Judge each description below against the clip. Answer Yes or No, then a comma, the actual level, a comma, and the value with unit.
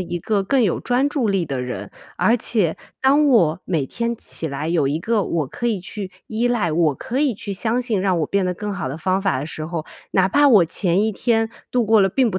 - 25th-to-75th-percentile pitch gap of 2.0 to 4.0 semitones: No, wide, 5.5 semitones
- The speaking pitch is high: Yes, high, 195 Hz